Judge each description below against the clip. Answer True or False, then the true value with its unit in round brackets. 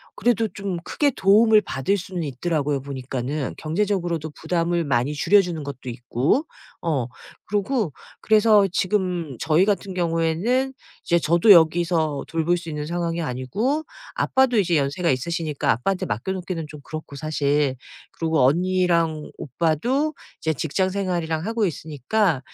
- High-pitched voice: False (170 Hz)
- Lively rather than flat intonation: False (4.6 semitones)